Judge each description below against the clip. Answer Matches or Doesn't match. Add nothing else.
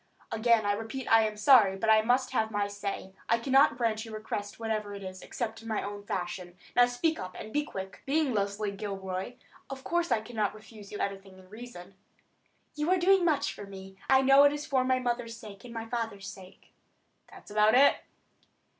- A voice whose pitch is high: Matches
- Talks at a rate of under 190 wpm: Doesn't match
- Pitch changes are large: Doesn't match